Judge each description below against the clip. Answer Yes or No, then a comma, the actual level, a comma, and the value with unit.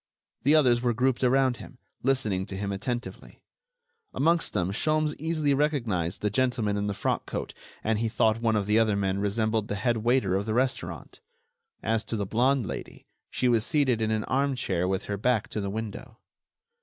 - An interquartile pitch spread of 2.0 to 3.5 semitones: No, average, 4.1 semitones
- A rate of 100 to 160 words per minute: No, average, 190 wpm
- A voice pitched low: Yes, low, 115 Hz